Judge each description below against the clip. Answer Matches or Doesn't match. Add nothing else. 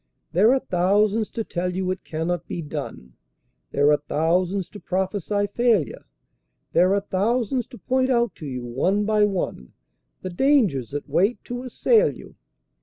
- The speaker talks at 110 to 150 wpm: Doesn't match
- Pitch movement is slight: Doesn't match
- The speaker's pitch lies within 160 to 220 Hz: Matches